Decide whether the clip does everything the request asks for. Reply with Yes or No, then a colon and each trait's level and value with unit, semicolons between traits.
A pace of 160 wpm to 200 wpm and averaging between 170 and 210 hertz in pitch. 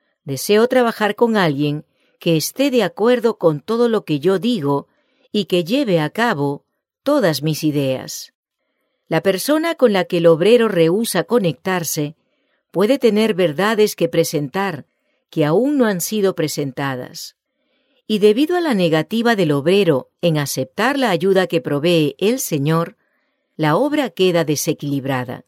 No: average, 145 wpm; medium, 185 Hz